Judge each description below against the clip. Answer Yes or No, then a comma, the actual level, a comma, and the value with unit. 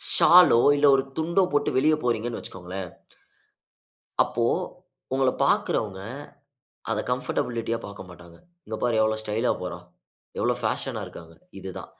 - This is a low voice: Yes, low, 115 Hz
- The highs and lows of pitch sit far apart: Yes, wide, 5.9 semitones